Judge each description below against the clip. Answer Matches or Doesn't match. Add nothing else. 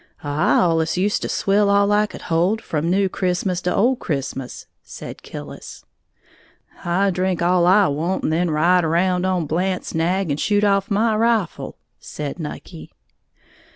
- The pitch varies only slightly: Doesn't match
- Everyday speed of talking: Matches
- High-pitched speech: Doesn't match